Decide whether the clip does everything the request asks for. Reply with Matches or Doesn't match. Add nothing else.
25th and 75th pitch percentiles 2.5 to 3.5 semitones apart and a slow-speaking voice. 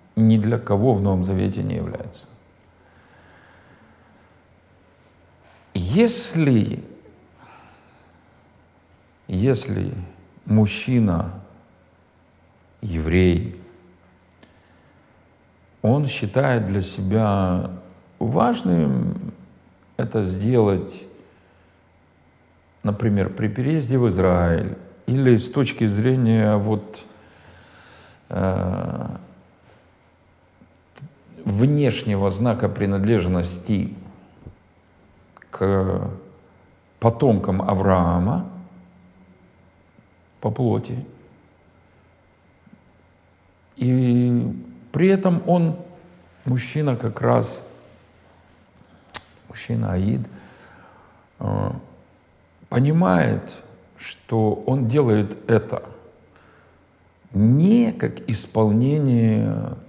Doesn't match